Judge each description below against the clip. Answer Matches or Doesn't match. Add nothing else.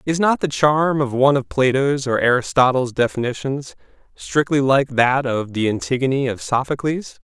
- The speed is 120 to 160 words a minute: Matches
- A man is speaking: Matches